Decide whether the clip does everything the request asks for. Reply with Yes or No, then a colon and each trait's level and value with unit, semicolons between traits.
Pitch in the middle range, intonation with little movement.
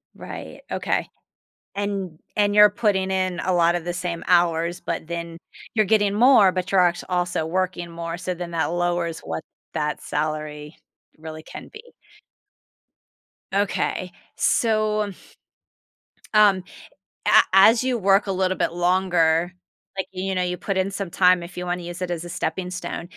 Yes: medium, 180 Hz; narrow, 2.2 semitones